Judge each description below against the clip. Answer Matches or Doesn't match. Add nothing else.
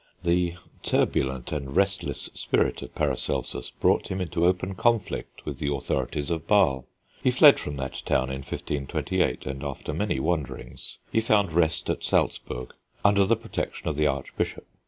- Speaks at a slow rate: Doesn't match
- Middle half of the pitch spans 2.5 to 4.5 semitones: Doesn't match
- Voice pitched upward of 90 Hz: Doesn't match